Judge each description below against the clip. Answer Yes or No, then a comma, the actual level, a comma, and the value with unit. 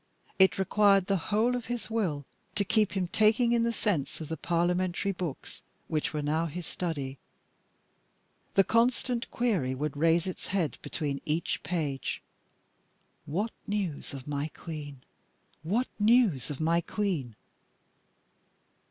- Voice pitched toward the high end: No, medium, 175 Hz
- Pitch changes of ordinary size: No, wide, 5.7 semitones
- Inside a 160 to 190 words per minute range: No, slow, 135 wpm